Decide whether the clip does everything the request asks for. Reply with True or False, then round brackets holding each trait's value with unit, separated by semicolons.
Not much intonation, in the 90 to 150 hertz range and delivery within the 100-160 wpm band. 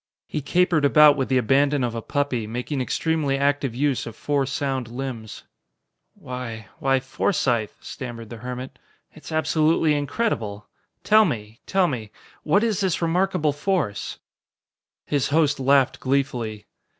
False (3.9 semitones; 135 Hz; 140 wpm)